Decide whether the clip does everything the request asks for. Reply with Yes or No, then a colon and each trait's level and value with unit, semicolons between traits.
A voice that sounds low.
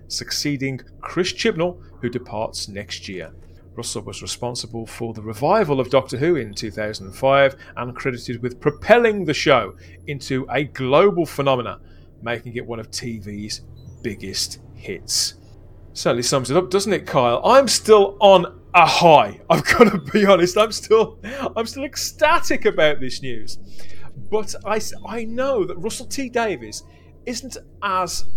Yes: low, 125 Hz